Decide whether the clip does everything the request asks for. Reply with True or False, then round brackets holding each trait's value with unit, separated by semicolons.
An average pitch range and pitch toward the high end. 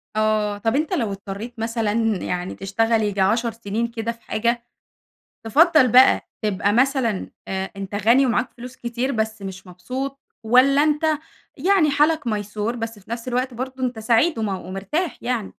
True (3.7 semitones; 230 Hz)